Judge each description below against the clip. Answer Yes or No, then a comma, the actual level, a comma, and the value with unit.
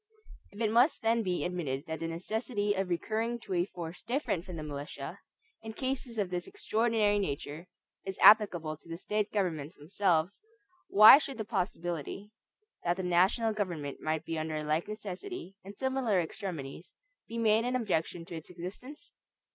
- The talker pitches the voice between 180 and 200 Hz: Yes, high, 190 Hz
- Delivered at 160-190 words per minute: Yes, average, 170 wpm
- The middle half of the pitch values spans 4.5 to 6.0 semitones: Yes, average, 4.9 semitones